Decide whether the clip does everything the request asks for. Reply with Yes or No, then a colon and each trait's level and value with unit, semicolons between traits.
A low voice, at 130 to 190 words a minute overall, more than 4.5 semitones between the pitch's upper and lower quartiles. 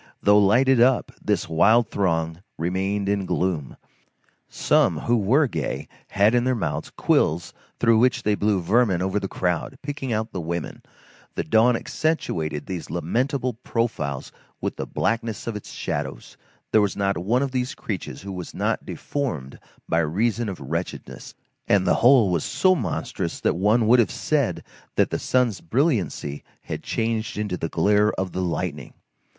Yes: low, 105 Hz; average, 165 wpm; average, 5.2 semitones